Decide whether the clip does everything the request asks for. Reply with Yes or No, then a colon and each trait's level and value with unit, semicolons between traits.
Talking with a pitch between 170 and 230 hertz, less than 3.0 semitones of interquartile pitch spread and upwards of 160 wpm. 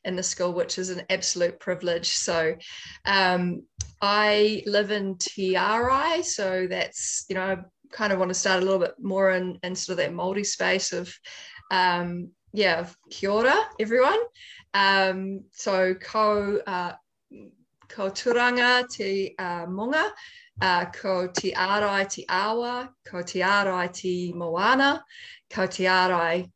No: high, 190 Hz; narrow, 2.6 semitones; average, 140 wpm